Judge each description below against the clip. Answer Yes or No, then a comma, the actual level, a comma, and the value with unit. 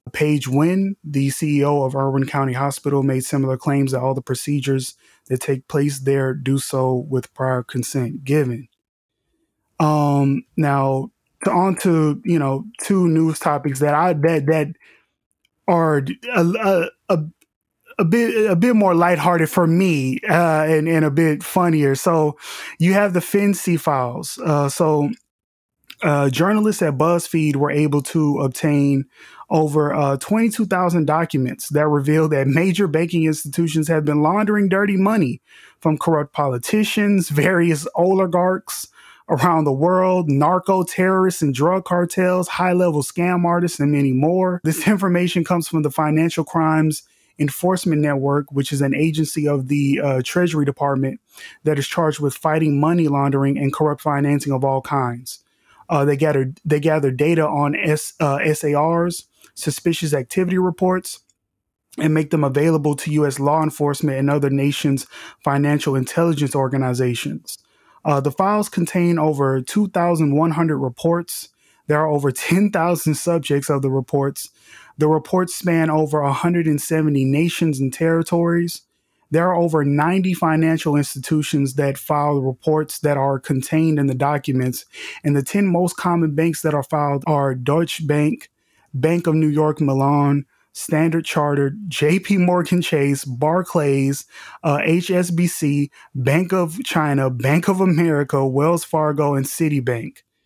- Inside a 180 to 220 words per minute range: No, average, 145 wpm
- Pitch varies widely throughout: No, average, 3.3 semitones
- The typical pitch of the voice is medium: Yes, medium, 155 Hz